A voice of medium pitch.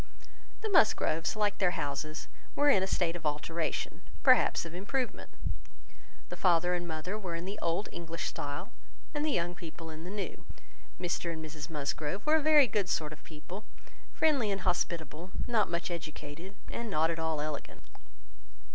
Yes: medium, 175 Hz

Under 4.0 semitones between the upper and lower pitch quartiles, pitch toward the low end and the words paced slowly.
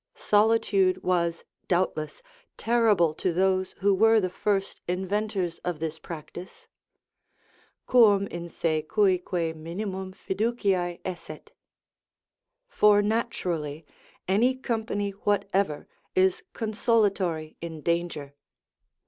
No: average, 3.4 semitones; high, 190 Hz; slow, 95 wpm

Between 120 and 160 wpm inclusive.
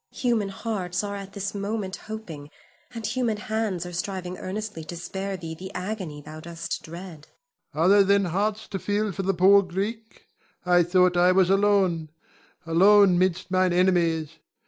No: average, 170 wpm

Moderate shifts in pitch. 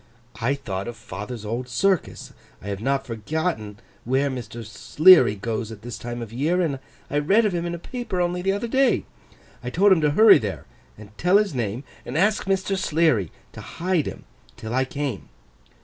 No: wide, 7.8 semitones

